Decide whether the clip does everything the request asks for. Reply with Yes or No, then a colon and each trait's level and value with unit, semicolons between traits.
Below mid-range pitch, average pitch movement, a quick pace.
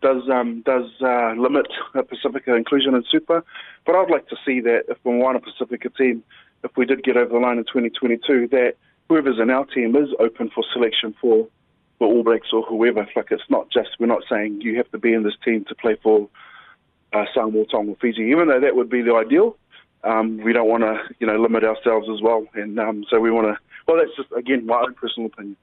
No: low, 115 Hz; narrow, 2.3 semitones; fast, 230 wpm